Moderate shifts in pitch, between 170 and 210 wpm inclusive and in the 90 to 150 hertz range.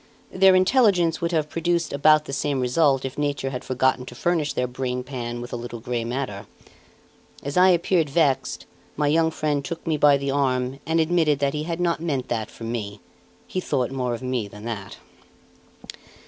Yes: average, 4.5 semitones; average, 190 wpm; medium, 140 Hz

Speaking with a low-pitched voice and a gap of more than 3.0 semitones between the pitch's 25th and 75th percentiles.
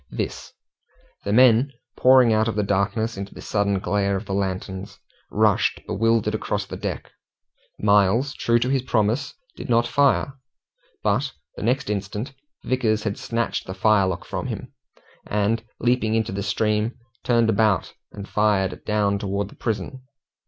No: low, 105 Hz; average, 2.7 semitones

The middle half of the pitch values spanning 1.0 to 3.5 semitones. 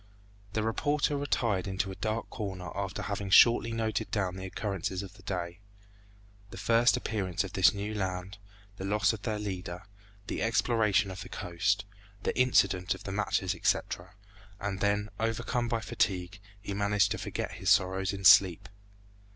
Yes: narrow, 2.5 semitones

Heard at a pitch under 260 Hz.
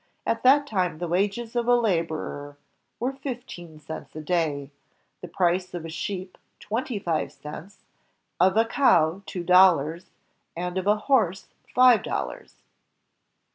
Yes: medium, 185 Hz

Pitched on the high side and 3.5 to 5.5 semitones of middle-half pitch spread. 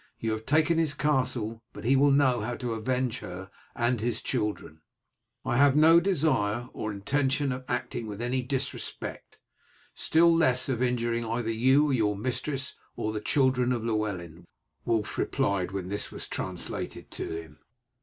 No: low, 120 Hz; average, 3.8 semitones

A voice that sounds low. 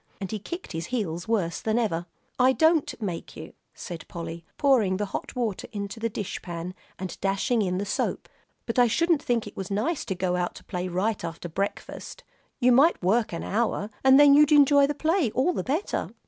No: high, 215 Hz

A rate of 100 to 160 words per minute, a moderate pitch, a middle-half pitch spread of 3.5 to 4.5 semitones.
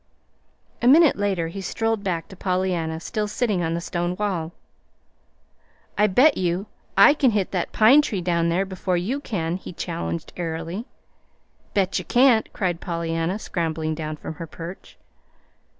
Yes: average, 155 wpm; medium, 180 Hz; average, 3.9 semitones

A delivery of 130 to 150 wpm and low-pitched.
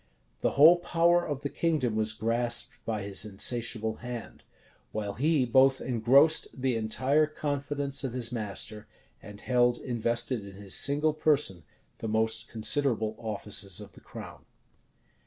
Yes: average, 140 wpm; low, 120 Hz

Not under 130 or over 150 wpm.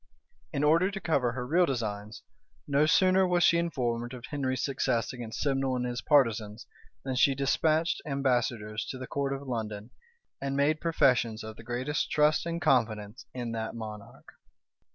No: average, 165 wpm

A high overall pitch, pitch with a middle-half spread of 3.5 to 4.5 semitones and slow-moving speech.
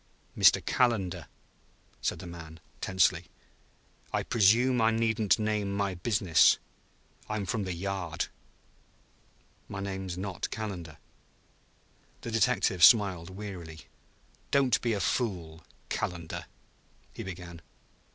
No: very low, 95 Hz; average, 4.0 semitones; slow, 110 wpm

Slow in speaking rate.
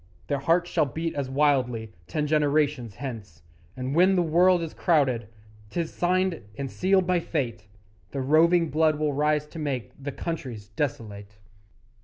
No: average, 155 wpm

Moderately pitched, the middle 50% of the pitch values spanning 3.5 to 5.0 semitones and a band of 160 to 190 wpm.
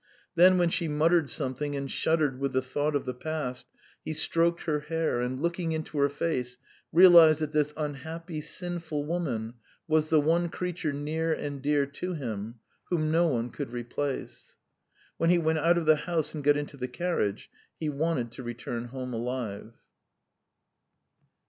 Yes: medium, 150 Hz; average, 4.0 semitones; average, 170 wpm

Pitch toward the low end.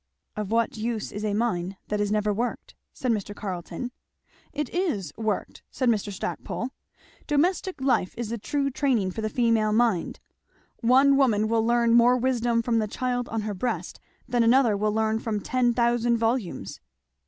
No: high, 230 Hz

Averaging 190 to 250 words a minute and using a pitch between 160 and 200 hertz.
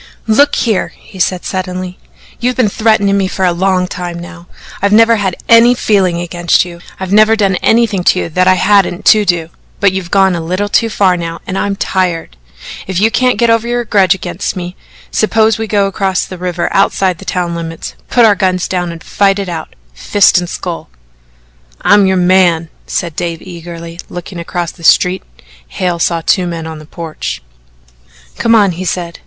Yes: average, 195 wpm; medium, 185 Hz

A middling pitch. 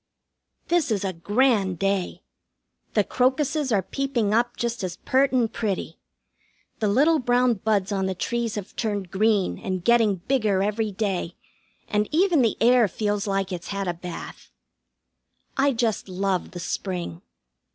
No: high, 210 Hz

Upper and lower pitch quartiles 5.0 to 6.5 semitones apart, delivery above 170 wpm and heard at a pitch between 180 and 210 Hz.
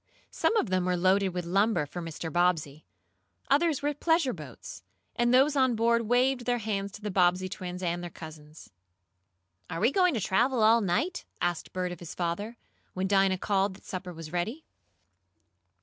Yes: average, 5.3 semitones; average, 180 wpm; high, 190 Hz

